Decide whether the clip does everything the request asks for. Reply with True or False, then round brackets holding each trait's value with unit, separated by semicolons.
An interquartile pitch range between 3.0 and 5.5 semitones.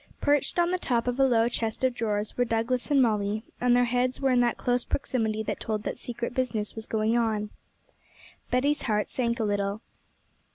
False (2.5 semitones)